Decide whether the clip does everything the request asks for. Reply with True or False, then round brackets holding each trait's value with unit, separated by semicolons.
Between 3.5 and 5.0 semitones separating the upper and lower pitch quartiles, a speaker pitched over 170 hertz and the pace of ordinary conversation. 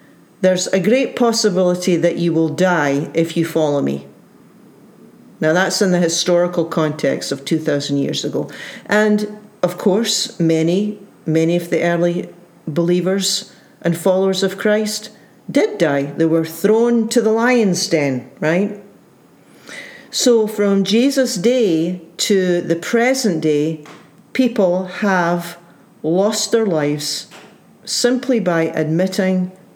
False (4.3 semitones; 185 Hz; 125 wpm)